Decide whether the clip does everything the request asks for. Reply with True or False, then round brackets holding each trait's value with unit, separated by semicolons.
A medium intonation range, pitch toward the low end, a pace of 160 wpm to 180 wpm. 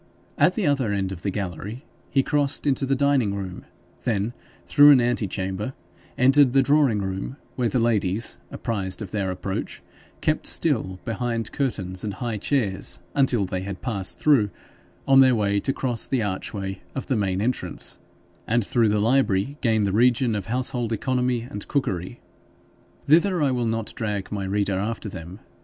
True (4.7 semitones; 115 Hz; 170 wpm)